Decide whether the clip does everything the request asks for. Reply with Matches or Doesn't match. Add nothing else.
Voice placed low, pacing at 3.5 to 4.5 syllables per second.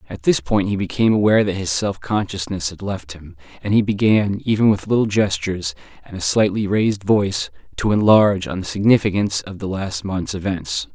Doesn't match